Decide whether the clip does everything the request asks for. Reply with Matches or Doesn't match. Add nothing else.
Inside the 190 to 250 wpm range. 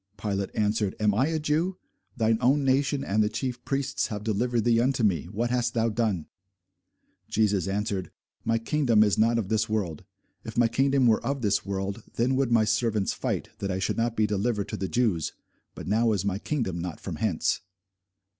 Matches